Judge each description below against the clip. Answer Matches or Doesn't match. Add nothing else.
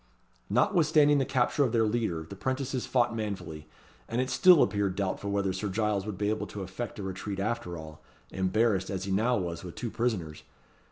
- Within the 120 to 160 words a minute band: Doesn't match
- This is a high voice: Doesn't match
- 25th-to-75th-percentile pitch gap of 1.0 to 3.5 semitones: Doesn't match